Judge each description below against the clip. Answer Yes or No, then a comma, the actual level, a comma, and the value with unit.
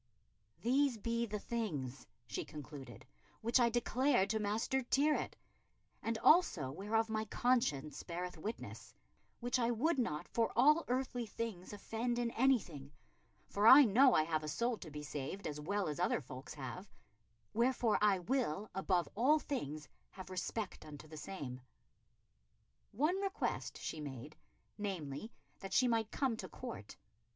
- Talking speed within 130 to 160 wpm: Yes, average, 150 wpm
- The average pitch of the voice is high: Yes, high, 210 Hz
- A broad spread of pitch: Yes, wide, 7.8 semitones